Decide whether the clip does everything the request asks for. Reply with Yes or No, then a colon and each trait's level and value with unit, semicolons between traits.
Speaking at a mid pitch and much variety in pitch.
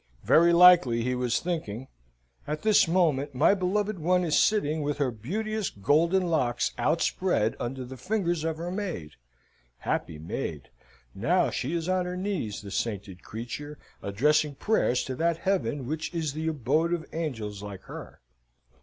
Yes: medium, 155 Hz; wide, 6.4 semitones